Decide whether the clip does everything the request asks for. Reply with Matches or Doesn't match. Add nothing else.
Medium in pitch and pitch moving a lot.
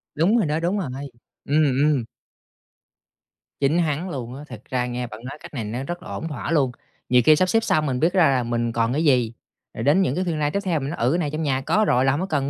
Doesn't match